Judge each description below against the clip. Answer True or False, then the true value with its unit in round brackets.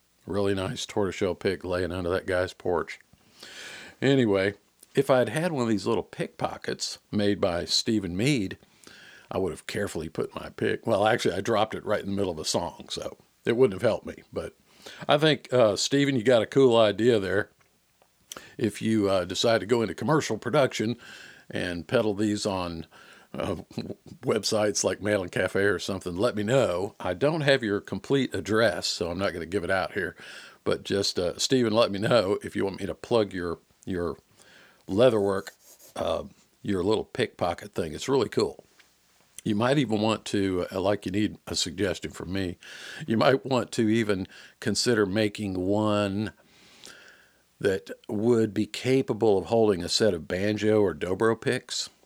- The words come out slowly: False (180 wpm)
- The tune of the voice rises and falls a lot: False (3.4 semitones)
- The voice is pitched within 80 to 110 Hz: True (105 Hz)